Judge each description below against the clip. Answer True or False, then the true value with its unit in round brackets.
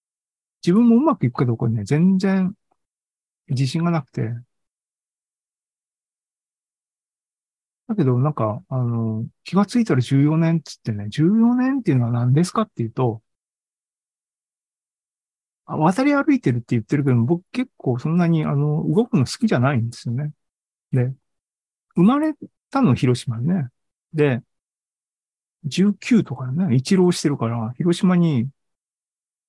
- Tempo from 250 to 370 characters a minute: False (240 characters per minute)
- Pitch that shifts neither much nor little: False (6.9 semitones)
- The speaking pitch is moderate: True (150 Hz)